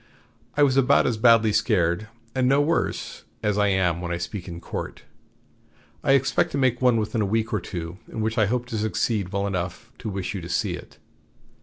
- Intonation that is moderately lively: Yes, average, 4.4 semitones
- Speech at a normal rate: No, fast, 210 wpm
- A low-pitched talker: Yes, low, 110 Hz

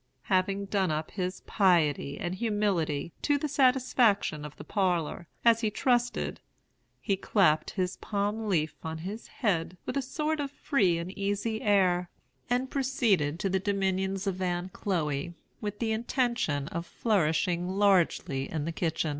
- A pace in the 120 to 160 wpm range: Yes, average, 155 wpm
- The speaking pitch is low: No, high, 190 Hz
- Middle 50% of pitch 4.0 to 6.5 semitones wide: Yes, average, 4.4 semitones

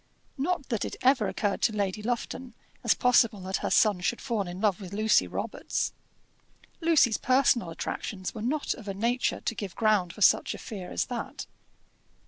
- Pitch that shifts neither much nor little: Yes, average, 3.9 semitones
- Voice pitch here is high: Yes, high, 220 Hz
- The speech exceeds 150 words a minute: Yes, average, 180 wpm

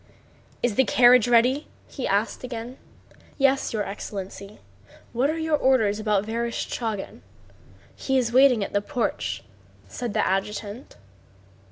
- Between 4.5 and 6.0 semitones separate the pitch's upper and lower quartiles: No, average, 4.0 semitones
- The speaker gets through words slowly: Yes, slow, 130 wpm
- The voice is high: Yes, high, 230 Hz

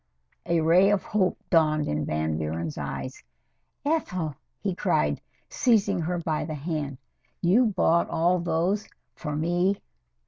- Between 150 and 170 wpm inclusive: No, slow, 135 wpm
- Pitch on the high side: No, medium, 165 Hz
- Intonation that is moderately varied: Yes, average, 3.8 semitones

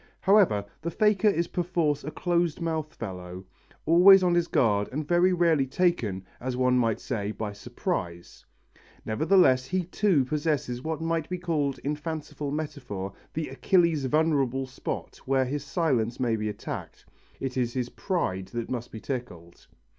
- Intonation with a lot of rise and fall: Yes, wide, 6.0 semitones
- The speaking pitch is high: No, medium, 140 Hz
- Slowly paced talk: No, average, 155 wpm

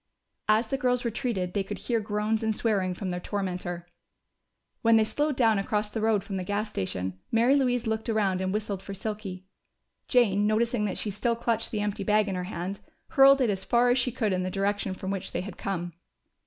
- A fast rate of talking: Yes, fast, 215 wpm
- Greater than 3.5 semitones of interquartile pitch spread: No, average, 3.2 semitones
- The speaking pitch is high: Yes, high, 210 Hz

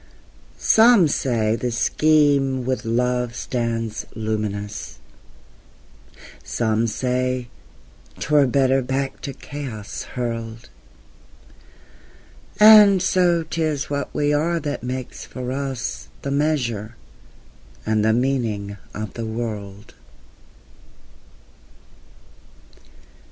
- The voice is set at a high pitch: No, low, 125 Hz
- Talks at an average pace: No, slow, 95 wpm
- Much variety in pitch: No, average, 4.1 semitones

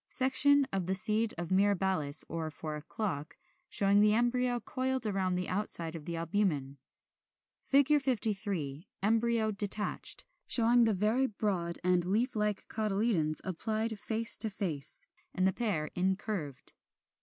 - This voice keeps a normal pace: No, slow, 130 wpm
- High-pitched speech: Yes, high, 205 Hz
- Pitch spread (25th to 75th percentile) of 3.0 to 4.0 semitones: No, average, 4.5 semitones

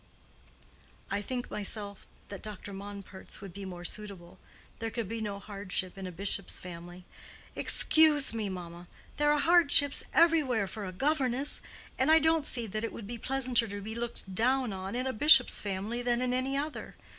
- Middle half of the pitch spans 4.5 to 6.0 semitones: Yes, average, 5.0 semitones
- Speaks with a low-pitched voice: No, high, 220 Hz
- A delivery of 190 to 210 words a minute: No, average, 180 wpm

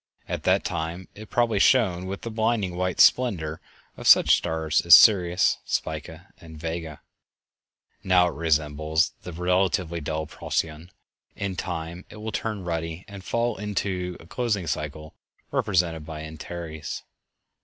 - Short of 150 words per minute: Yes, average, 140 wpm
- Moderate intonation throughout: Yes, average, 3.6 semitones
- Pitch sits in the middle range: No, very low, 85 Hz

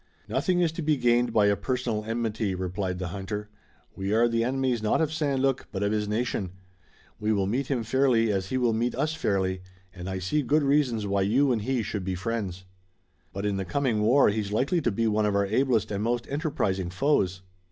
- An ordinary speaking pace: No, fast, 215 wpm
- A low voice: Yes, low, 110 Hz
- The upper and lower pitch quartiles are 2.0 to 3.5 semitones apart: No, average, 4.7 semitones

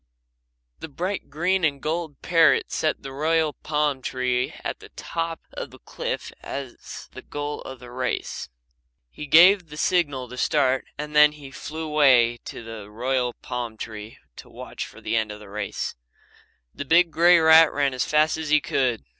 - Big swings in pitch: No, average, 4.1 semitones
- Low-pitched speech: No, medium, 145 Hz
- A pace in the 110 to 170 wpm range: No, average, 180 wpm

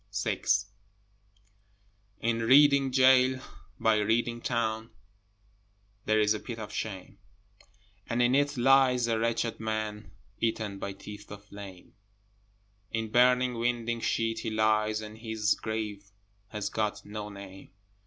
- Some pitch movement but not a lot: No, narrow, 2.2 semitones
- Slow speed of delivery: Yes, slow, 125 wpm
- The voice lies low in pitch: Yes, low, 110 Hz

